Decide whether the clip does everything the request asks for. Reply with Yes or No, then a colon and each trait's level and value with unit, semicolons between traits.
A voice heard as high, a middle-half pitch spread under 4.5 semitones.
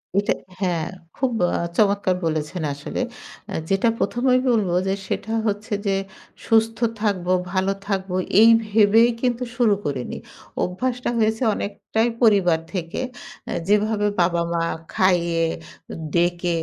Yes: high, 200 Hz; average, 4.0 semitones